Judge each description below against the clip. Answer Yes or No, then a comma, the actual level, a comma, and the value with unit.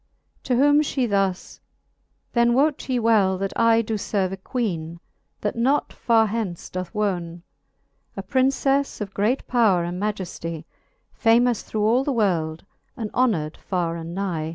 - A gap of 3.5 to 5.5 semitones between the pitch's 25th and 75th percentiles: Yes, average, 4.8 semitones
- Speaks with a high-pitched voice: Yes, high, 210 Hz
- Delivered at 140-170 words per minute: Yes, average, 150 wpm